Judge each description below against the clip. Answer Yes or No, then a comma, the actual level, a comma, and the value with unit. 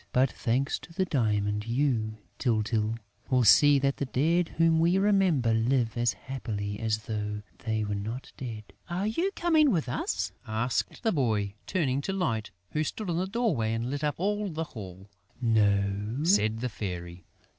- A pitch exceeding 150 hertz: No, low, 125 Hz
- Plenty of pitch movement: Yes, wide, 7.1 semitones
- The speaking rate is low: No, average, 170 wpm